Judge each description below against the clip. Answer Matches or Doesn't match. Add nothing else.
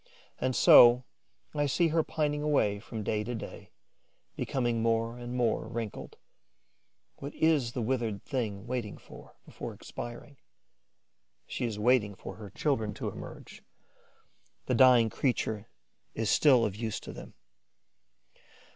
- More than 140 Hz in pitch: Doesn't match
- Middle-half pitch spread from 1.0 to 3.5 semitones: Matches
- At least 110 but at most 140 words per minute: Matches